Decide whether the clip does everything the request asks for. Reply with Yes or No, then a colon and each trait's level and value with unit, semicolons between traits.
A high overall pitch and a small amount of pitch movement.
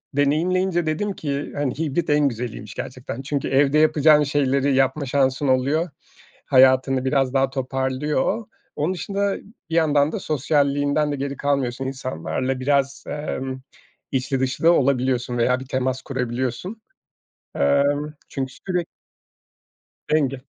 No: medium, 140 Hz; narrow, 2.3 semitones